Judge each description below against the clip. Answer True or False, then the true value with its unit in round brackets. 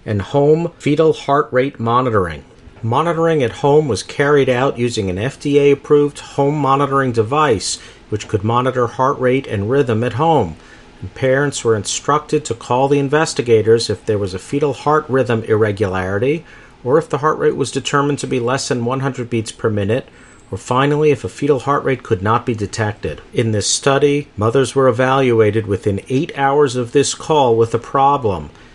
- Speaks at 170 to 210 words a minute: True (175 wpm)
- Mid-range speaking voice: False (130 Hz)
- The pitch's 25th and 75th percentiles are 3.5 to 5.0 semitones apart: True (4.1 semitones)